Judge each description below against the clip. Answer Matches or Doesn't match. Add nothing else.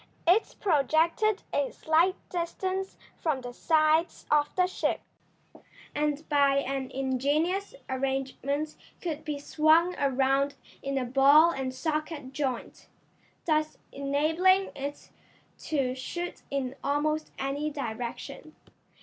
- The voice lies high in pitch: Matches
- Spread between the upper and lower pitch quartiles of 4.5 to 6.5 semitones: Doesn't match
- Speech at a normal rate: Doesn't match